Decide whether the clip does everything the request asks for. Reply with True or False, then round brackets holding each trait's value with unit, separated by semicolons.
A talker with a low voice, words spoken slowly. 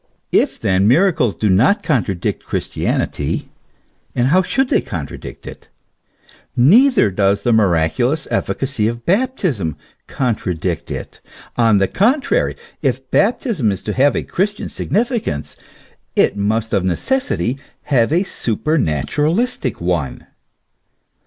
True (125 Hz; 120 wpm)